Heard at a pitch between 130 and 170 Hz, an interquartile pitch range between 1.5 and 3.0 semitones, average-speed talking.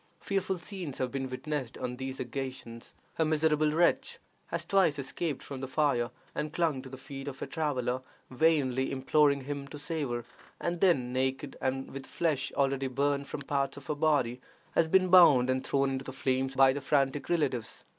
Yes: medium, 140 Hz; average, 2.7 semitones; average, 190 wpm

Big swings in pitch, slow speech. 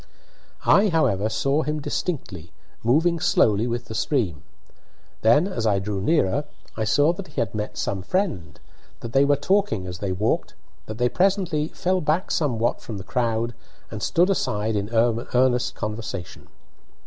No: wide, 6.9 semitones; average, 160 wpm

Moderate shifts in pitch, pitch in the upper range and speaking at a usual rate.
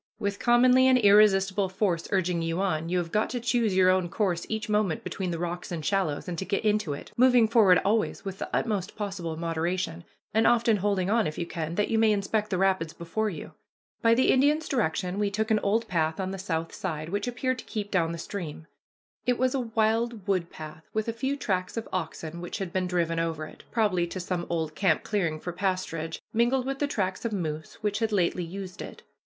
No: average, 4.3 semitones; high, 195 Hz; fast, 220 wpm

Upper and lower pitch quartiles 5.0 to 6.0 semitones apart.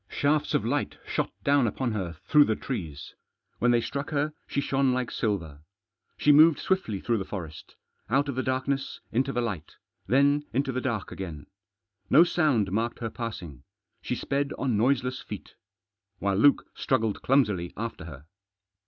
Yes: wide, 5.5 semitones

